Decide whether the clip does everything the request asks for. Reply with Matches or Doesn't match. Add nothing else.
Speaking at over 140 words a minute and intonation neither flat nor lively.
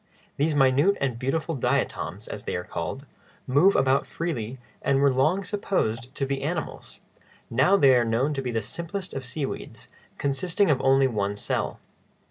Matches